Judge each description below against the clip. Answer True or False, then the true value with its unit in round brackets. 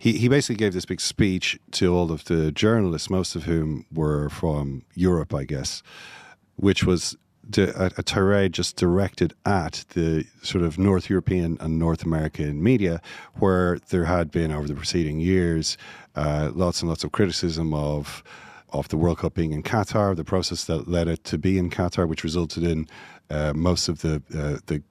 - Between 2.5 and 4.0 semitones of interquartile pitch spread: True (2.8 semitones)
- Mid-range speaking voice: False (85 Hz)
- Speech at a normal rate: True (190 wpm)